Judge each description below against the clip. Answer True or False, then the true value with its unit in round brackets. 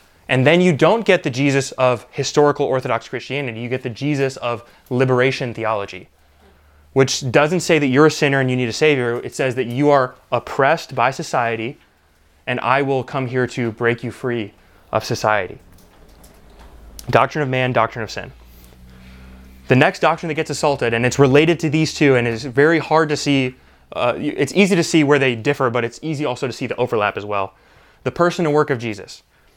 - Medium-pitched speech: False (130 Hz)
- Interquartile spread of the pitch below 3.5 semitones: False (4.4 semitones)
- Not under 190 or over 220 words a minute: True (195 wpm)